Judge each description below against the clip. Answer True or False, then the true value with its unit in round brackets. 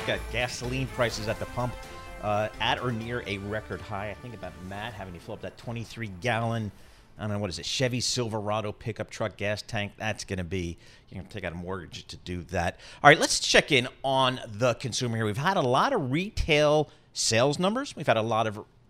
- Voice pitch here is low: True (110 Hz)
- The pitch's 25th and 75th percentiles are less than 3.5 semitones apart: False (3.8 semitones)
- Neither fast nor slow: False (230 wpm)